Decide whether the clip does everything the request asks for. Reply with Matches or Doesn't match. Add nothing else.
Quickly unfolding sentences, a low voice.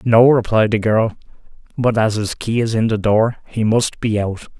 Matches